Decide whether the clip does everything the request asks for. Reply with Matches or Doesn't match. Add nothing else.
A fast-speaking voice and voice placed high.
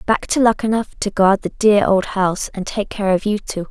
Matches